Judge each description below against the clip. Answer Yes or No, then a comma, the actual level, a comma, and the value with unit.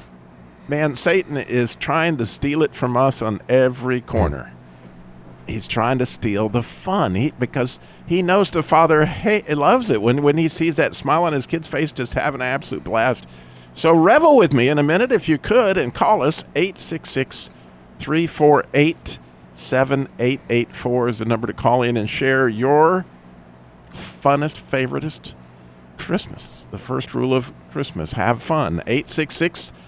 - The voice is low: Yes, low, 125 Hz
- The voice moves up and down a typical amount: No, wide, 8.9 semitones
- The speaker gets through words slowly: No, average, 155 wpm